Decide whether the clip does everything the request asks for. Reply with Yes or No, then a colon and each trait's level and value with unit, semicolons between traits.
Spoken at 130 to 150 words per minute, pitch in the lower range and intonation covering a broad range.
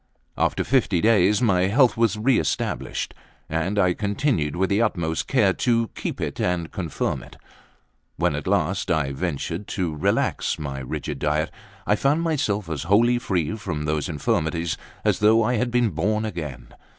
No: average, 165 wpm; very low, 95 Hz; wide, 5.9 semitones